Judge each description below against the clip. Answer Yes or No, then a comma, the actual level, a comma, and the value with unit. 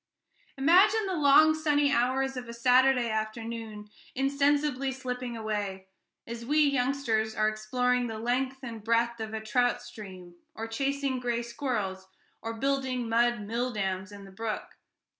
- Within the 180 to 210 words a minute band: No, average, 140 wpm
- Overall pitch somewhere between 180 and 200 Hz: No, high, 240 Hz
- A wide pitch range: No, average, 3.5 semitones